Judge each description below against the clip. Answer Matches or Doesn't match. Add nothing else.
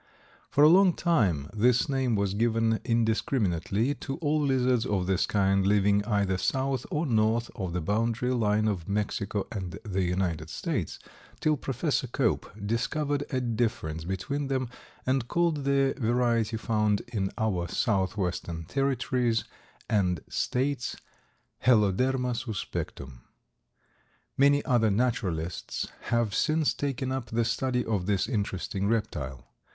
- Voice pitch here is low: Matches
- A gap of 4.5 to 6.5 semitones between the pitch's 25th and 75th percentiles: Matches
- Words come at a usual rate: Doesn't match